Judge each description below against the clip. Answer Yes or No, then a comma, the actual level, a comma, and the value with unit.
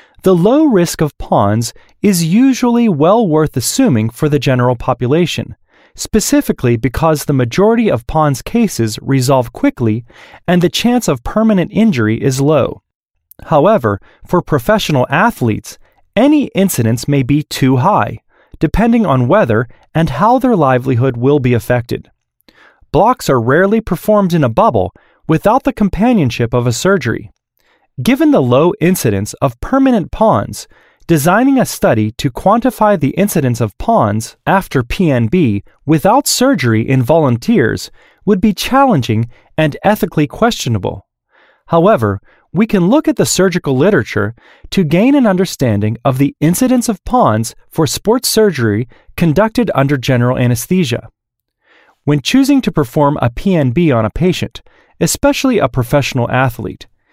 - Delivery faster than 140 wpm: No, slow, 135 wpm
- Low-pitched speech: No, medium, 155 Hz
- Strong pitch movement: Yes, wide, 8.8 semitones